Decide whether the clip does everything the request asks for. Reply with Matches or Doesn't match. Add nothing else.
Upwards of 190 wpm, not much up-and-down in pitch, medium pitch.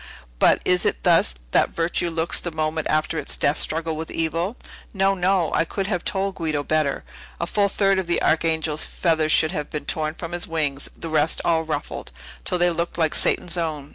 Matches